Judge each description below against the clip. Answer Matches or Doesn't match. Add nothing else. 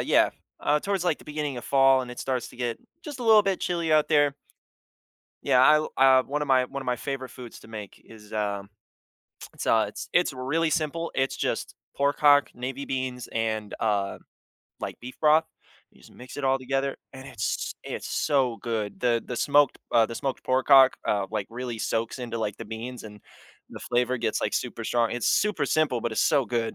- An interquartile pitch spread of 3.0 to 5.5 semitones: Matches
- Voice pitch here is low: Matches